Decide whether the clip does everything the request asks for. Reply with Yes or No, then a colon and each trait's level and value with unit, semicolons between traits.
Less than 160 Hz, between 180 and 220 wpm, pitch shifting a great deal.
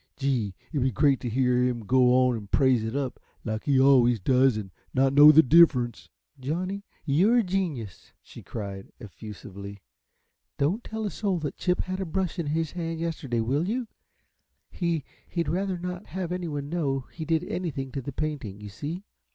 Yes: medium, 140 Hz; average, 185 wpm; wide, 5.7 semitones